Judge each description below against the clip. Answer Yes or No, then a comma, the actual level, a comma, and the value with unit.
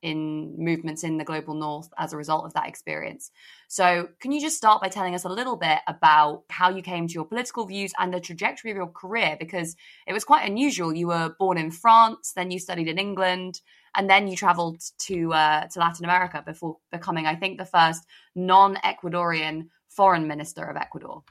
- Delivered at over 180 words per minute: Yes, fast, 205 wpm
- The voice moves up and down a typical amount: Yes, average, 3.2 semitones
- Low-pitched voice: No, medium, 175 Hz